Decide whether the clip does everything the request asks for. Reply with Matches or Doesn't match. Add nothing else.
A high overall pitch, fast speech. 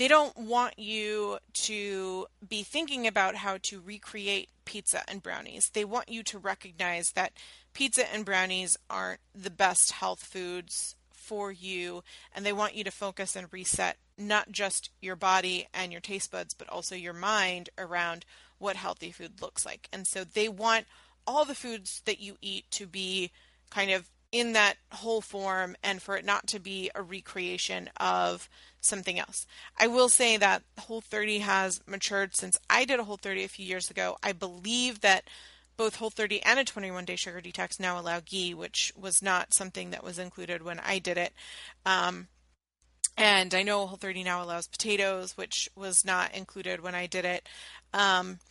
Doesn't match